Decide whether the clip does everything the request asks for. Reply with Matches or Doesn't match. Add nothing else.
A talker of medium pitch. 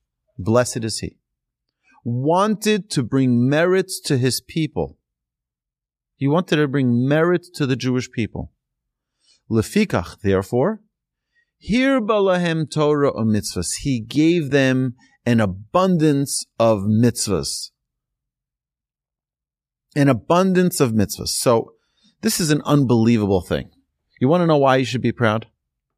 Doesn't match